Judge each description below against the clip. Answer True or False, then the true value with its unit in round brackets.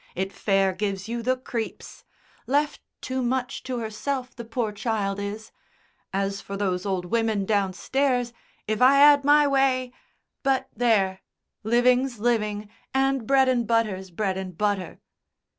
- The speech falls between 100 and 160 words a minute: True (140 wpm)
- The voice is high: True (225 Hz)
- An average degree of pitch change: True (4.5 semitones)